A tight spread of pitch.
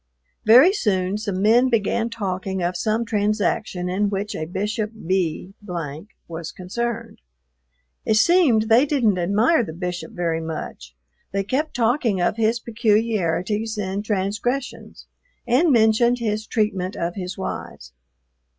No: average, 3.8 semitones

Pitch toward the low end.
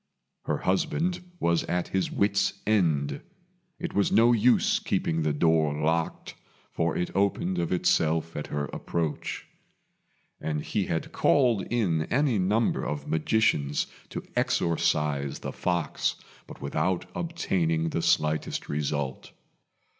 Yes: very low, 85 Hz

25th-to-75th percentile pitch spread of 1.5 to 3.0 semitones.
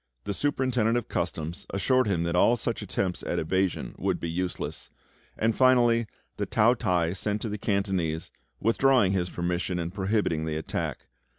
No: average, 4.8 semitones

